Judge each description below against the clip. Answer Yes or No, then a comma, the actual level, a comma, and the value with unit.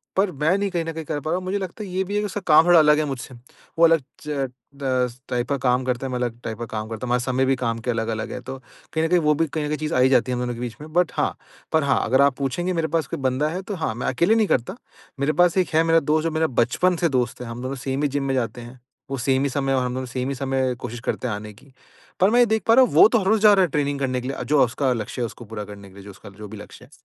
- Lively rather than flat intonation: No, average, 4.8 semitones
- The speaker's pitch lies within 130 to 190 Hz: Yes, low, 135 Hz